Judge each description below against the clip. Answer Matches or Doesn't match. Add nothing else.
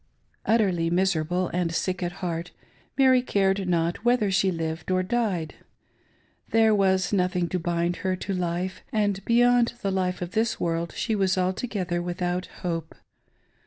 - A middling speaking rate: Matches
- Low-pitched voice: Doesn't match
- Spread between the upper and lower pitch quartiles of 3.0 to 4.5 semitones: Doesn't match